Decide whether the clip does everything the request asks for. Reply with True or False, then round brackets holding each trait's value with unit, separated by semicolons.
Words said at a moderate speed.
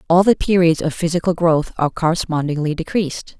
True (160 wpm)